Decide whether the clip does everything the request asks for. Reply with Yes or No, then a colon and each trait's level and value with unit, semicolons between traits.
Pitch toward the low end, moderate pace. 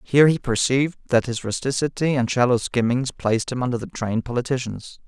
Yes: low, 125 Hz; average, 175 wpm